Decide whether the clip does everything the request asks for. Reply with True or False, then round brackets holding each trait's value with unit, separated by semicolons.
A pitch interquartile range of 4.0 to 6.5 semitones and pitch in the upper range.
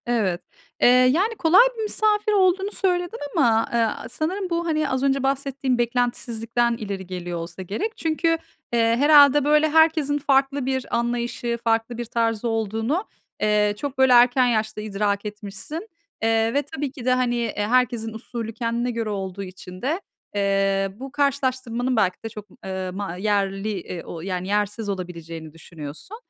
True (5.3 semitones; 235 Hz)